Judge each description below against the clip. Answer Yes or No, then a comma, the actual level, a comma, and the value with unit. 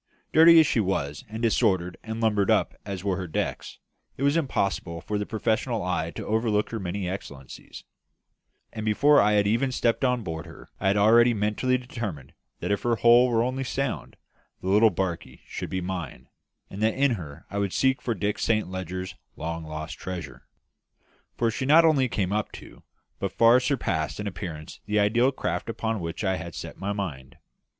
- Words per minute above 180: Yes, average, 190 wpm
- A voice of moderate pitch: No, low, 105 Hz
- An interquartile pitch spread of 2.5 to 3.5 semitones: No, average, 4.5 semitones